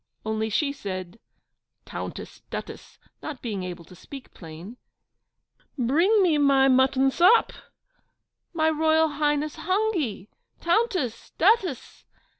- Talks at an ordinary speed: No, slow, 105 wpm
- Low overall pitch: No, very high, 280 Hz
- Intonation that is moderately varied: No, wide, 7.0 semitones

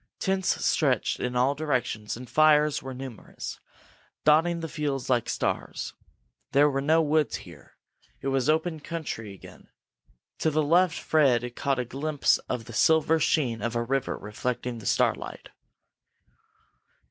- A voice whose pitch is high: No, medium, 140 Hz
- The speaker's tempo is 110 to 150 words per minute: Yes, average, 145 wpm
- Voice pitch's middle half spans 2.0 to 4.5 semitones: Yes, average, 4.0 semitones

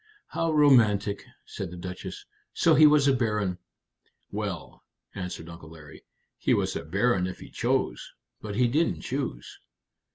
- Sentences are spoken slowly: No, average, 150 wpm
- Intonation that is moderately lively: No, wide, 7.0 semitones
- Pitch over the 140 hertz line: No, low, 105 Hz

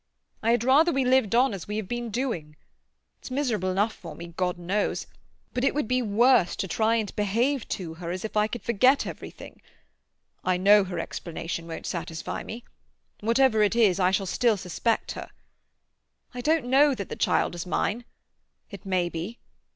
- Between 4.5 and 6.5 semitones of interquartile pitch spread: Yes, average, 5.1 semitones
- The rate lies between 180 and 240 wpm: Yes, average, 185 wpm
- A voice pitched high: Yes, high, 210 Hz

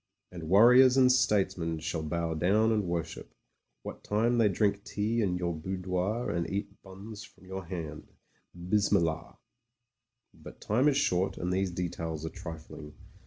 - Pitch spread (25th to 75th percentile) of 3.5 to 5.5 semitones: Yes, average, 4.0 semitones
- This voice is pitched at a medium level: No, very low, 95 Hz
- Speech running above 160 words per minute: No, average, 155 wpm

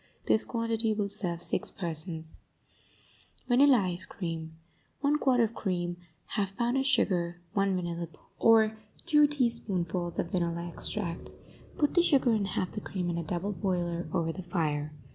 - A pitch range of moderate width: Yes, average, 4.8 semitones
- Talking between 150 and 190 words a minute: Yes, average, 160 wpm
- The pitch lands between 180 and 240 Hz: Yes, medium, 185 Hz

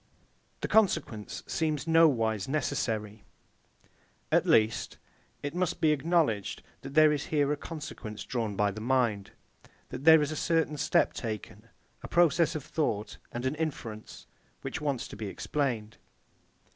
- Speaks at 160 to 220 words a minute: No, average, 145 wpm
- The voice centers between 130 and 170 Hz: Yes, medium, 140 Hz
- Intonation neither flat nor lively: No, wide, 6.1 semitones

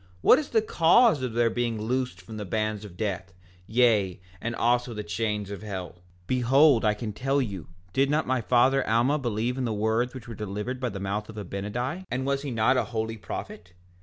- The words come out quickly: Yes, fast, 210 wpm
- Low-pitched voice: Yes, low, 115 Hz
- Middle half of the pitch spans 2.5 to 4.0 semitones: Yes, average, 3.5 semitones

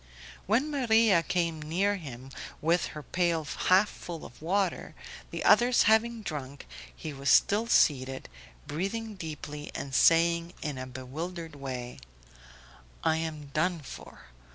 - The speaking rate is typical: No, slow, 130 wpm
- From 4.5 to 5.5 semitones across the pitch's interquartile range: Yes, average, 5.2 semitones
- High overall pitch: No, medium, 165 Hz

